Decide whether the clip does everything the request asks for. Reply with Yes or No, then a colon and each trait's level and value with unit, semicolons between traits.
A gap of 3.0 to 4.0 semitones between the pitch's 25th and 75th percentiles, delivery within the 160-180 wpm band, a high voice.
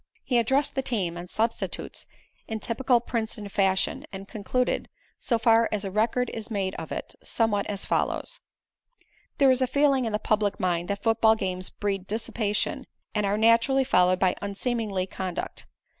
Yes: average, 3.4 semitones; average, 165 wpm; high, 215 Hz